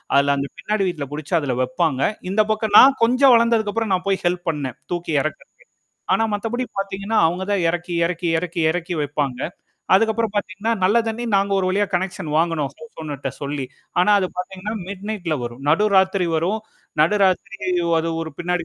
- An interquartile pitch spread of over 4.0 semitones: Yes, average, 4.4 semitones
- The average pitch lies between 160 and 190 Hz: Yes, medium, 185 Hz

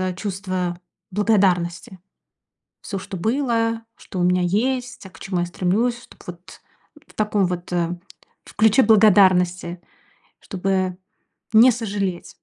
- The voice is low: No, high, 190 Hz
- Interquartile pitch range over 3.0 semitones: Yes, average, 3.5 semitones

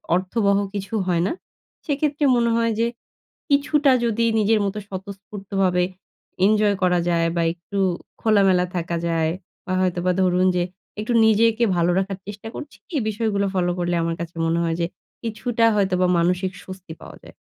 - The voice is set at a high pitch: Yes, high, 195 Hz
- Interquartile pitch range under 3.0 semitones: No, average, 3.6 semitones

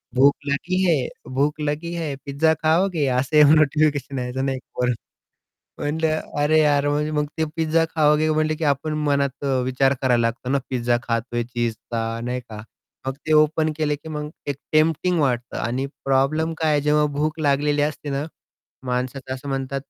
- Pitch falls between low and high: Yes, medium, 145 Hz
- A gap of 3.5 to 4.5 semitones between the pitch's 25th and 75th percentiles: No, average, 2.9 semitones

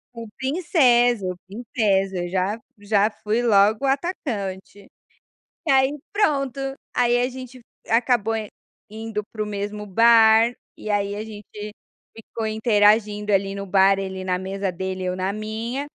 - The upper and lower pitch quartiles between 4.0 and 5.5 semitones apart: No, average, 3.4 semitones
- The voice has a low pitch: No, high, 215 Hz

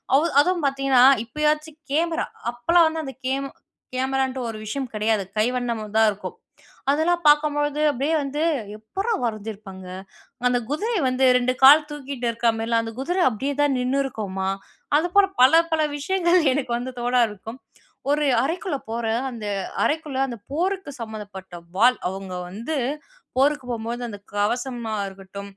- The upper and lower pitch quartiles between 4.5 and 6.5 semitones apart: Yes, average, 5.0 semitones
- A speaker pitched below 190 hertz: No, very high, 260 Hz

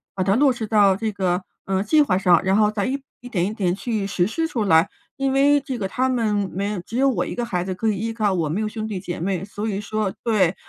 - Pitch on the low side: No, high, 210 Hz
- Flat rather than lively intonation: No, average, 3.3 semitones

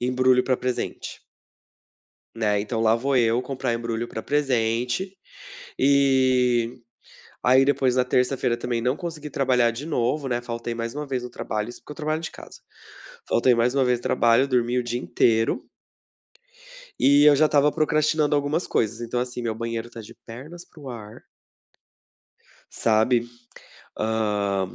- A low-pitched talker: Yes, low, 125 Hz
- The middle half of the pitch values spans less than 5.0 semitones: Yes, average, 3.0 semitones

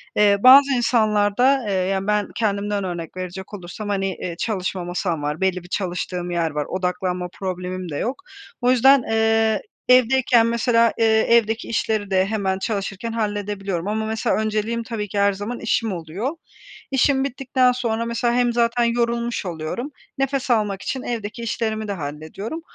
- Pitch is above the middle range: Yes, high, 215 Hz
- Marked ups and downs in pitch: No, average, 3.7 semitones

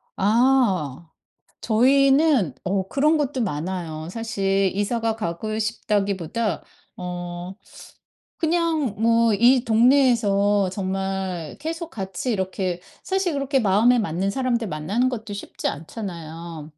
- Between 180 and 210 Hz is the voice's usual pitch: Yes, high, 205 Hz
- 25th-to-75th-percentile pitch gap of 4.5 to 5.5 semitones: Yes, average, 5.1 semitones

